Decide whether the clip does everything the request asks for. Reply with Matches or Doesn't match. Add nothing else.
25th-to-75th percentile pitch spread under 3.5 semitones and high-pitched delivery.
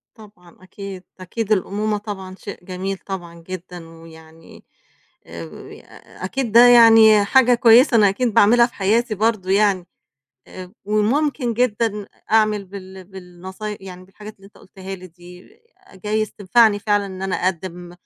Matches